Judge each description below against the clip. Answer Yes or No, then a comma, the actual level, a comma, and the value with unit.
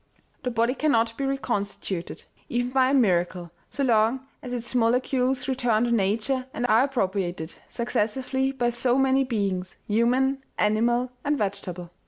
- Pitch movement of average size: Yes, average, 3.9 semitones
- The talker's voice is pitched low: No, high, 240 Hz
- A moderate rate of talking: Yes, average, 150 wpm